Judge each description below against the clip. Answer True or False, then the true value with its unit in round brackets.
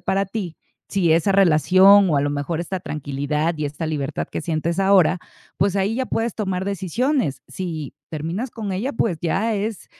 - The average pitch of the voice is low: False (185 Hz)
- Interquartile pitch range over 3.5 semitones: True (4.2 semitones)